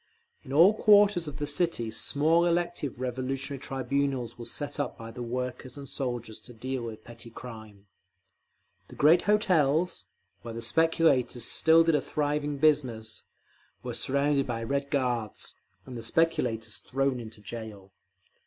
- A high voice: No, low, 135 Hz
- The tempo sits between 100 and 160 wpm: Yes, average, 145 wpm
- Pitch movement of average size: Yes, average, 4.3 semitones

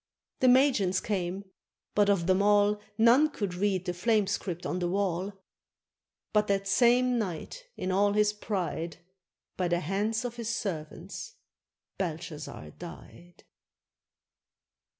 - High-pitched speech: Yes, high, 200 Hz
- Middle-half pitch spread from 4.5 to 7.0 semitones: No, average, 3.2 semitones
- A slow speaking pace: Yes, slow, 130 wpm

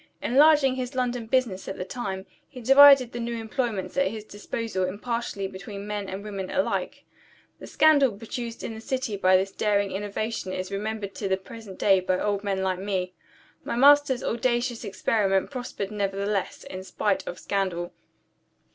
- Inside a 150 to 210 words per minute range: Yes, average, 165 wpm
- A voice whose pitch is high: Yes, high, 210 Hz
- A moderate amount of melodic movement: Yes, average, 3.9 semitones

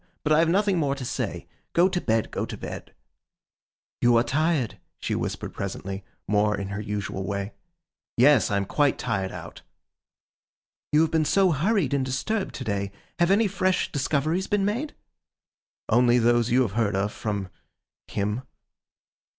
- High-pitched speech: No, low, 130 Hz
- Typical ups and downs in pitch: No, wide, 8.2 semitones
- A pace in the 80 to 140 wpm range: No, average, 160 wpm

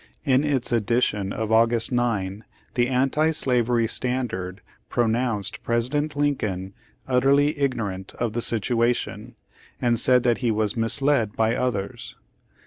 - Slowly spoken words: Yes, slow, 125 wpm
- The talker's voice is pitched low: Yes, low, 120 Hz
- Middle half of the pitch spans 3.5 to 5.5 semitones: No, average, 2.7 semitones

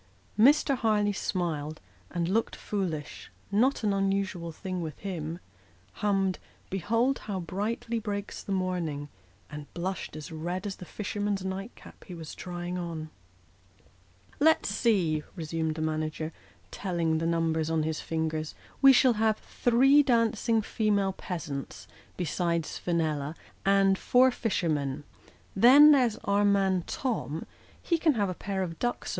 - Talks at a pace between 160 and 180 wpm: No, average, 145 wpm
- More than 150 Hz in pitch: Yes, high, 190 Hz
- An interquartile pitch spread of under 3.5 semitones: No, average, 4.7 semitones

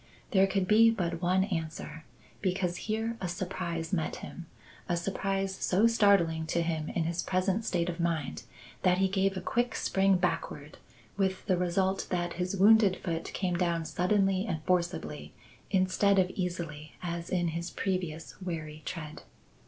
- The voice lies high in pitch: No, medium, 180 Hz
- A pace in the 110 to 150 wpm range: No, average, 160 wpm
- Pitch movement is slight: Yes, narrow, 2.3 semitones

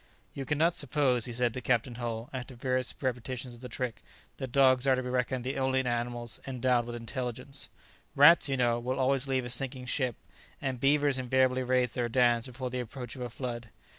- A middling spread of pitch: No, narrow, 1.6 semitones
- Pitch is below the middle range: Yes, low, 125 Hz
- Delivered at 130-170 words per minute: No, average, 200 wpm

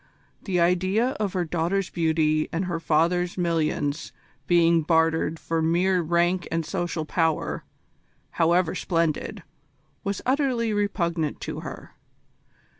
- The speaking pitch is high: No, medium, 170 Hz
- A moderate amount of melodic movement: No, narrow, 2.2 semitones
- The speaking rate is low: Yes, slow, 115 wpm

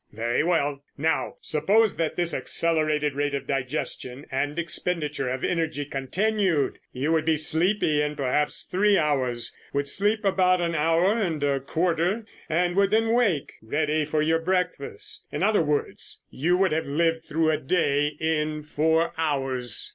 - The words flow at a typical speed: Yes, average, 155 wpm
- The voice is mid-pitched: Yes, medium, 155 Hz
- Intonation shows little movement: No, average, 3.5 semitones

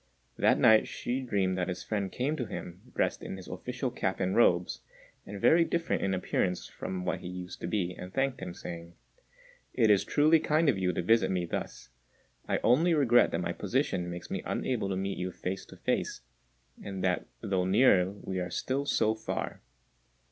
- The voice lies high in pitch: No, very low, 95 Hz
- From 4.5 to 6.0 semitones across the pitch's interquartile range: Yes, average, 5.2 semitones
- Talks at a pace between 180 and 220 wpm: Yes, average, 195 wpm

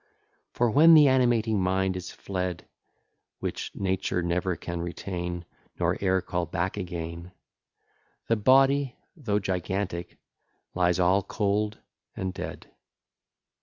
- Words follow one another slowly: Yes, slow, 115 wpm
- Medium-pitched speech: No, very low, 95 Hz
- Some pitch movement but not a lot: Yes, average, 3.3 semitones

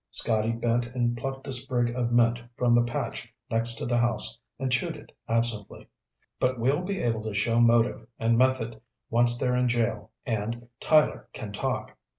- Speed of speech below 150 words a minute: No, average, 175 wpm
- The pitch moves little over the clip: Yes, narrow, 1.4 semitones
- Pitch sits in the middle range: No, low, 120 Hz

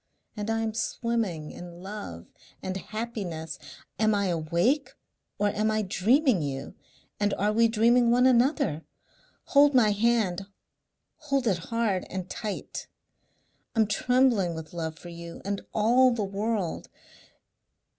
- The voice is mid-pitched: No, high, 210 Hz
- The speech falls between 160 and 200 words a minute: No, slow, 135 wpm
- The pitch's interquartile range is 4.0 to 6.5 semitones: Yes, average, 4.7 semitones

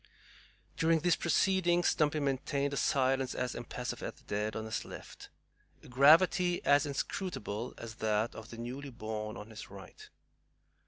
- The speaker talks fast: No, average, 155 wpm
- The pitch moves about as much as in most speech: No, wide, 5.7 semitones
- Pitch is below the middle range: Yes, low, 130 Hz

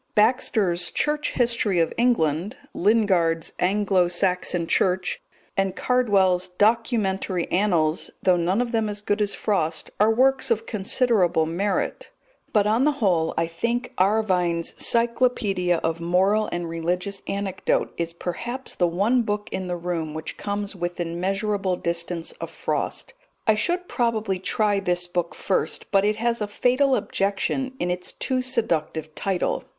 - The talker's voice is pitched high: Yes, high, 195 Hz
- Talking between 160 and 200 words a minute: No, average, 145 wpm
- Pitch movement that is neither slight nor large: Yes, average, 4.1 semitones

